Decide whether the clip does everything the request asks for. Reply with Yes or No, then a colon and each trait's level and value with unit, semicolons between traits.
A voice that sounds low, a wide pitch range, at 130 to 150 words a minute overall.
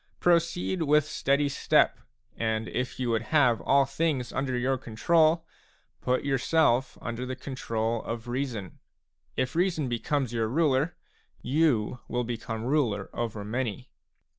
No: low, 130 Hz; average, 4.1 semitones; average, 140 wpm